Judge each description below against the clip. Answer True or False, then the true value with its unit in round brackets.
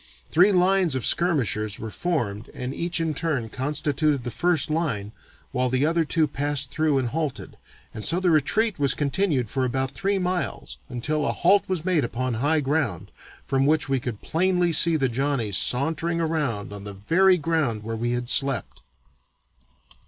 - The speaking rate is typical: True (175 wpm)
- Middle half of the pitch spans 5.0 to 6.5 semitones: True (5.3 semitones)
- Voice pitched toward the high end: False (145 Hz)